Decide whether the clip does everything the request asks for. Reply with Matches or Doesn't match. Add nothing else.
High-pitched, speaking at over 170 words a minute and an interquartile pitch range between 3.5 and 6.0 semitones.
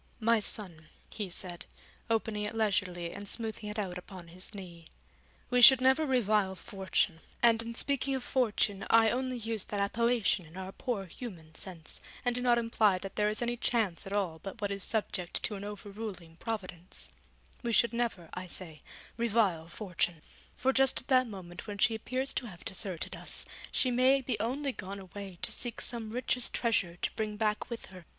Matches